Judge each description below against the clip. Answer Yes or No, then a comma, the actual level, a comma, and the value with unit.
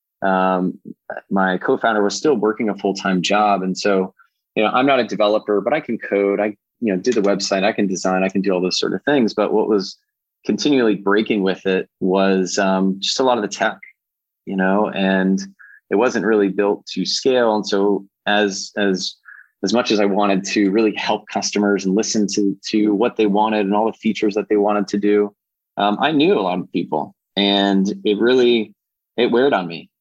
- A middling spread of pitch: No, narrow, 1.7 semitones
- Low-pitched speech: Yes, low, 100 Hz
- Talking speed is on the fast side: Yes, fast, 210 wpm